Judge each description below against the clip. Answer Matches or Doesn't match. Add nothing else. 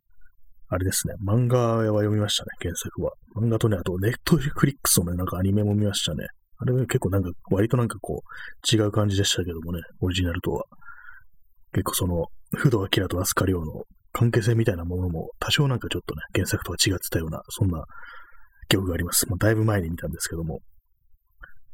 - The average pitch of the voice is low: Matches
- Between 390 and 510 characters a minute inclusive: Matches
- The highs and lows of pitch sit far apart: Doesn't match